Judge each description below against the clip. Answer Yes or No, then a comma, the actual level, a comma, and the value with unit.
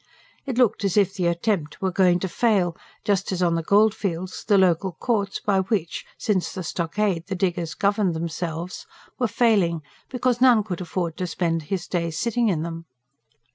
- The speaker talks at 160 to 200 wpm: Yes, average, 175 wpm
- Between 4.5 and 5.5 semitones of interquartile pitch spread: No, average, 3.4 semitones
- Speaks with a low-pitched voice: No, medium, 185 Hz